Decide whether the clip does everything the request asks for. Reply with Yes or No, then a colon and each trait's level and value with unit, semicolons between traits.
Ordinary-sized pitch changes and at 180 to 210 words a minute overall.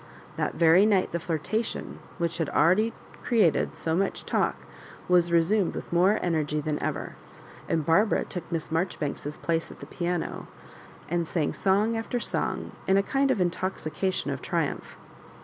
No: average, 3.3 semitones; average, 160 wpm